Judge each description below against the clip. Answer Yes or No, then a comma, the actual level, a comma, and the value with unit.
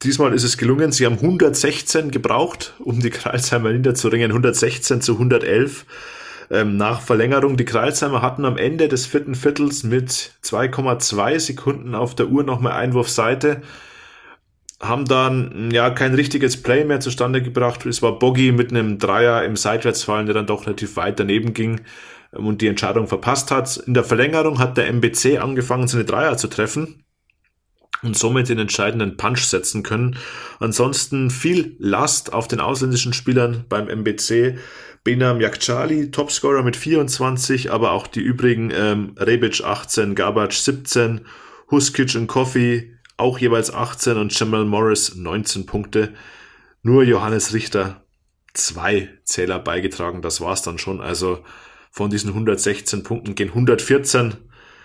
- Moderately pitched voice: No, low, 120 Hz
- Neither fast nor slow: Yes, average, 145 wpm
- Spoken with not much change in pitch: No, average, 3.1 semitones